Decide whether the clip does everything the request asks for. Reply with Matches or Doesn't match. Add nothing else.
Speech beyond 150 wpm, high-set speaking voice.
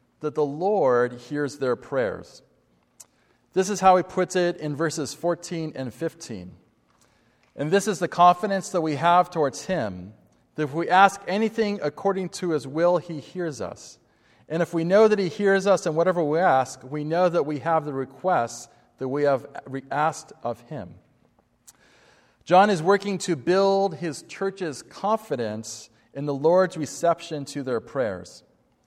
Doesn't match